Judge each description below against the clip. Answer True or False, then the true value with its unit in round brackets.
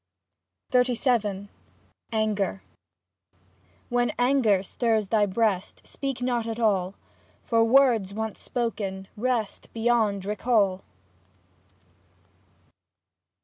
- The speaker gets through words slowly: True (80 wpm)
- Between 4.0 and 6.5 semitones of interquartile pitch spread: False (3.2 semitones)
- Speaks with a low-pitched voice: False (220 Hz)